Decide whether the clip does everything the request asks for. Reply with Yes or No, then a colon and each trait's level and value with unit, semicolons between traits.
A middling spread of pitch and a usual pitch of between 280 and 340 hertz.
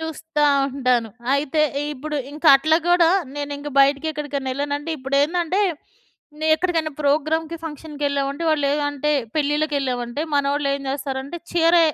No: narrow, 2.1 semitones; very high, 290 Hz